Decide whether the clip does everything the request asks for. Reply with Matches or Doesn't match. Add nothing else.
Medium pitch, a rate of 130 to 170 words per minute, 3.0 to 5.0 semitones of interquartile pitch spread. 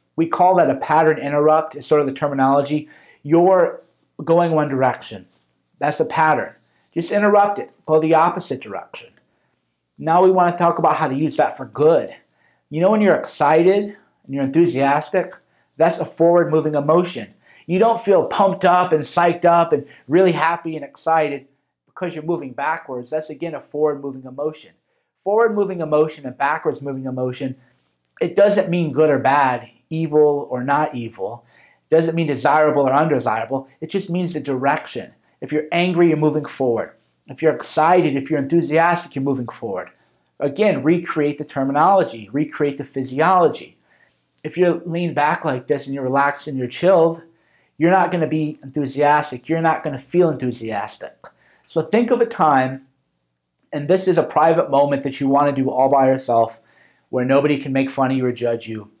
Doesn't match